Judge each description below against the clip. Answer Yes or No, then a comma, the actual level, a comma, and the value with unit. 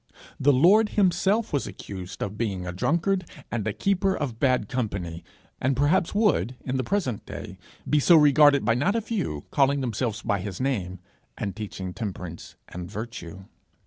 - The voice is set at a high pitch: No, low, 125 Hz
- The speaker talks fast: No, average, 170 wpm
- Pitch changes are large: Yes, wide, 7.9 semitones